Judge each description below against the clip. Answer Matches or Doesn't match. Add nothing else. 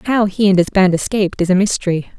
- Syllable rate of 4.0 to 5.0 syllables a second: Doesn't match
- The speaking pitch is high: Matches